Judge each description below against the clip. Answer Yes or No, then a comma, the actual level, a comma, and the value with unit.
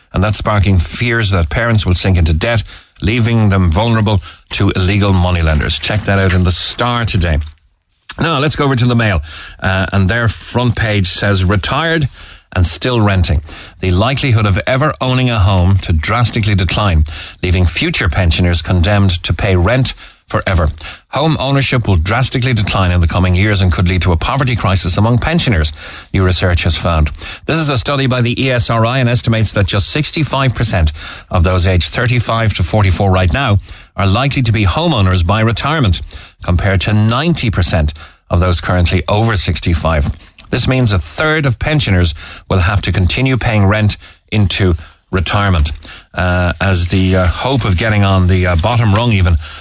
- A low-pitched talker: Yes, very low, 95 Hz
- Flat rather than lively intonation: No, average, 4.5 semitones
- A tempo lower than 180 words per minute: Yes, average, 170 wpm